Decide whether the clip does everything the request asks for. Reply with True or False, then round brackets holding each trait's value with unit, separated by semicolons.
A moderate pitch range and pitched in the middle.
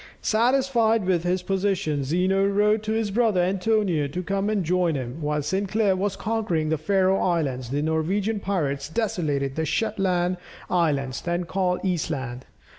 True (4.5 semitones; 180 Hz)